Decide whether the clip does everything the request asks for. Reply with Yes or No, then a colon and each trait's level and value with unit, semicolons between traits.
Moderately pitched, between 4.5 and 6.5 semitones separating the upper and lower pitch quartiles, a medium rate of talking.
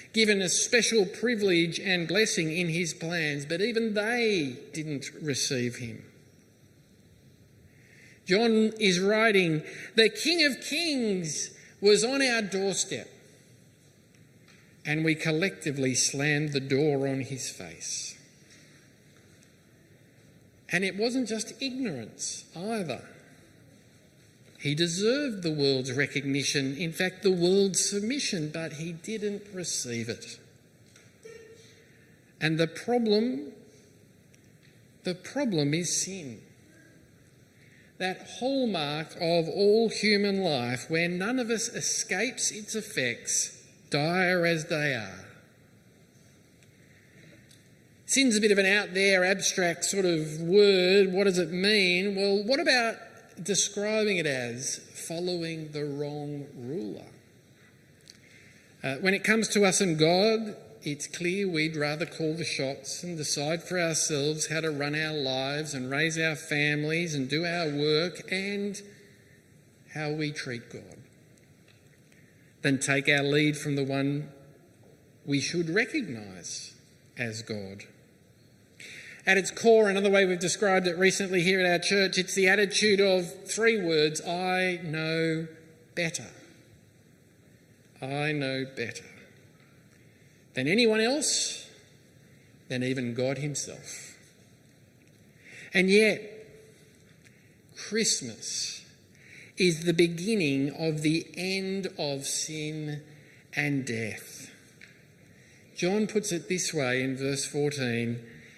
No: medium, 165 Hz; wide, 5.6 semitones; slow, 115 wpm